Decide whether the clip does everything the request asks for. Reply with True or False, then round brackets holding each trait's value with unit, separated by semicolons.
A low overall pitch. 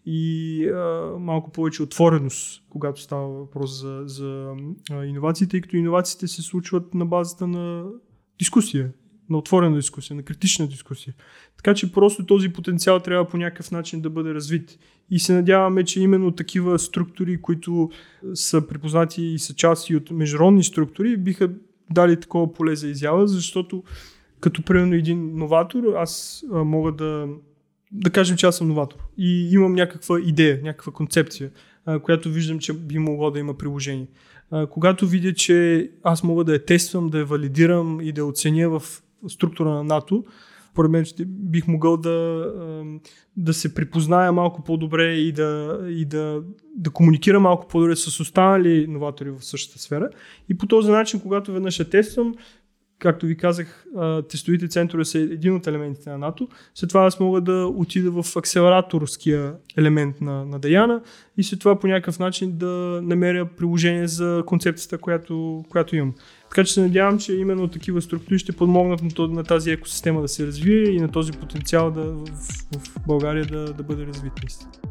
False (165 Hz)